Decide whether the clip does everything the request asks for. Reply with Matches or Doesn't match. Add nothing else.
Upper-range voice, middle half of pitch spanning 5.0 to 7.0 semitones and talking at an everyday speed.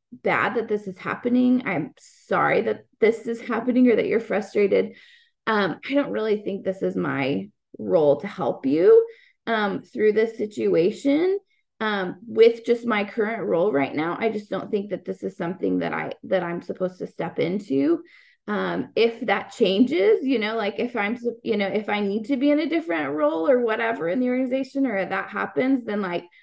Matches